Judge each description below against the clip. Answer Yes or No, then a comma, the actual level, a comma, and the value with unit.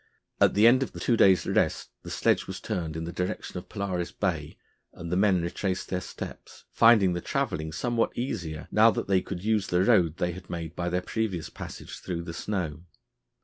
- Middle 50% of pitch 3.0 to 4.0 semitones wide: Yes, average, 3.5 semitones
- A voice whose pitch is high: No, very low, 90 Hz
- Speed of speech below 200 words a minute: No, fast, 205 wpm